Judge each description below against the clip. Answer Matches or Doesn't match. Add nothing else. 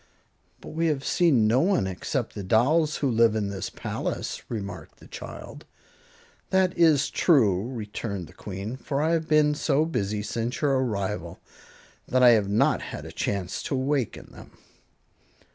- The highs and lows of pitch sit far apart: Matches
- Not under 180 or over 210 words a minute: Doesn't match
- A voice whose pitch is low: Matches